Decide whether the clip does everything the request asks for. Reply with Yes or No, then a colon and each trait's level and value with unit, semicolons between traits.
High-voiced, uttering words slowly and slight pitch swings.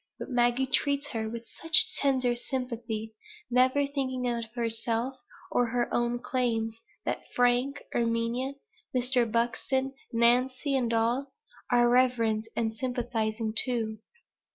Yes: high, 240 Hz; slow, 120 wpm; narrow, 2.0 semitones